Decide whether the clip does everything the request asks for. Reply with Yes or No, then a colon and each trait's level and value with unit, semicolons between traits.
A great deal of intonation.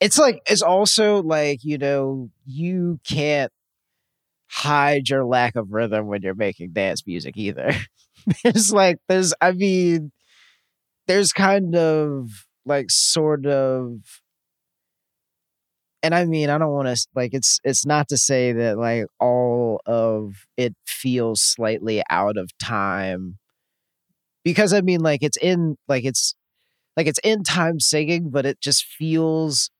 Yes: wide, 5.9 semitones